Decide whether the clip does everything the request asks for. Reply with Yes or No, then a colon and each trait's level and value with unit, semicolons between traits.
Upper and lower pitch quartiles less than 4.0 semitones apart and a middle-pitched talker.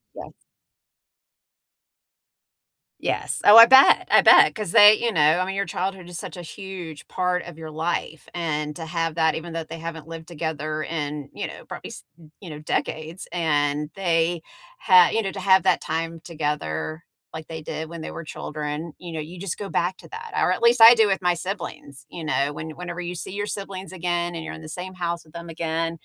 Yes: average, 2.7 semitones; medium, 170 Hz